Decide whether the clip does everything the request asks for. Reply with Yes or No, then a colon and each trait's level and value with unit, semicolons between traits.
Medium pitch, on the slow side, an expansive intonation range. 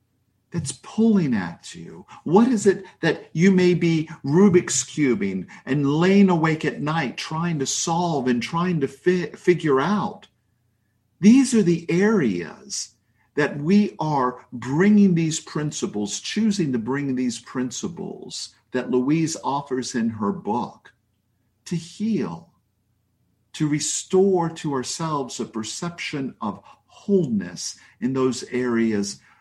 Yes: medium, 150 Hz; slow, 125 wpm; wide, 6.7 semitones